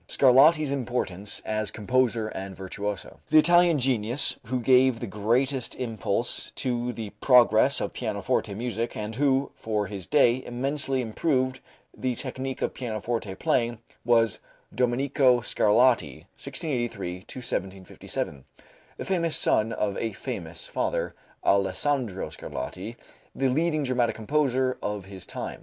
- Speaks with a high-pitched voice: No, low, 120 Hz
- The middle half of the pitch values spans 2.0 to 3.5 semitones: No, average, 3.9 semitones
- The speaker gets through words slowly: Yes, slow, 125 wpm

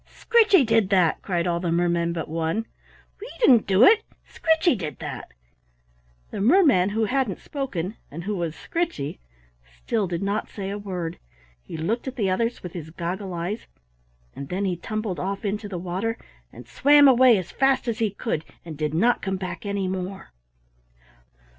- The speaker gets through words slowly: No, average, 175 wpm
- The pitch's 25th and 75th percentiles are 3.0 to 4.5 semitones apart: No, average, 5.0 semitones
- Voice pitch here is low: No, high, 195 Hz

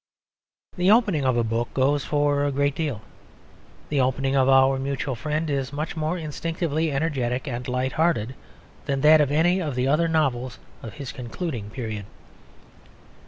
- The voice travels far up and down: No, average, 3.4 semitones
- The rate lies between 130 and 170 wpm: Yes, average, 165 wpm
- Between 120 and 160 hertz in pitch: Yes, medium, 140 Hz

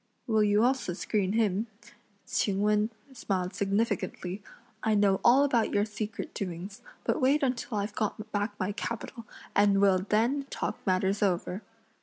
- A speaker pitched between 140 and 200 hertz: No, high, 210 Hz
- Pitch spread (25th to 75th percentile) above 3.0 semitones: No, narrow, 2.5 semitones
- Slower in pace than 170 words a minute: Yes, average, 150 wpm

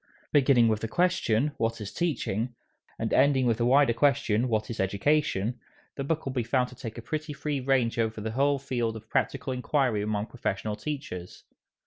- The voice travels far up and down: No, average, 4.0 semitones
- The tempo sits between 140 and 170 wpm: No, average, 185 wpm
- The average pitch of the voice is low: Yes, low, 125 Hz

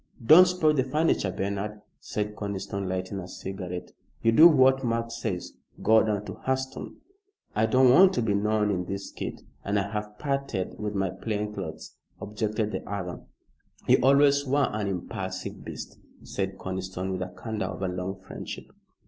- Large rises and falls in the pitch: No, average, 4.3 semitones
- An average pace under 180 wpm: Yes, average, 170 wpm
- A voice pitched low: Yes, low, 105 Hz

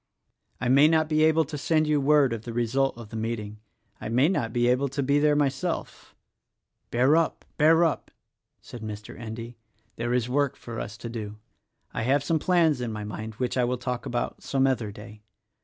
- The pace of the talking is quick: Yes, fast, 220 wpm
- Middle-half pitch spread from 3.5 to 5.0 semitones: Yes, average, 4.2 semitones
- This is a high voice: No, low, 125 Hz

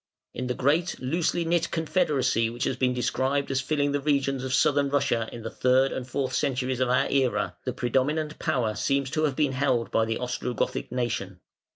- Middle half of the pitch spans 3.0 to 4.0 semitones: No, narrow, 2.5 semitones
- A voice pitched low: Yes, low, 130 Hz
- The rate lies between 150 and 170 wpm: No, average, 195 wpm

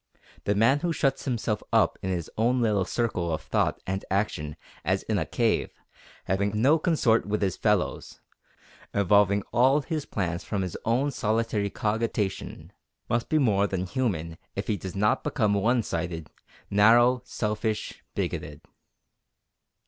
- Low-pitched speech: Yes, low, 105 Hz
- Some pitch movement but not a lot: Yes, average, 3.8 semitones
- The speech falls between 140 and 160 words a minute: Yes, average, 150 wpm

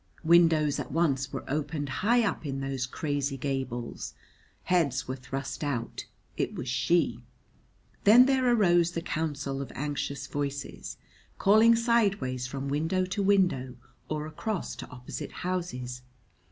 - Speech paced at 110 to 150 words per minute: Yes, slow, 135 wpm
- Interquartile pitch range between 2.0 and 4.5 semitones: No, average, 5.2 semitones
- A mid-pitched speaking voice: Yes, medium, 145 Hz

